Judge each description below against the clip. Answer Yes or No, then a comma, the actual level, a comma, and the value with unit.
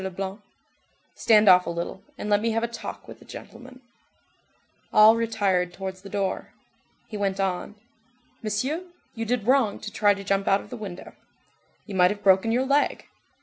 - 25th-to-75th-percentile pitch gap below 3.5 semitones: Yes, average, 2.9 semitones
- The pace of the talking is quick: No, average, 180 wpm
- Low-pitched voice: No, high, 205 Hz